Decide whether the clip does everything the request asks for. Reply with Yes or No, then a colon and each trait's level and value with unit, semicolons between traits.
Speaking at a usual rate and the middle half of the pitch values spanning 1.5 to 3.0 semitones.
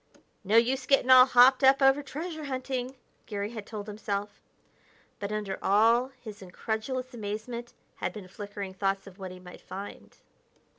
No: average, 155 wpm; average, 4.2 semitones